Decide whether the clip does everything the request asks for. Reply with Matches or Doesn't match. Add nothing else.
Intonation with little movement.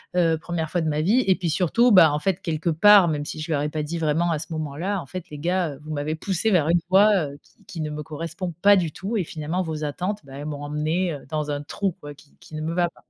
Doesn't match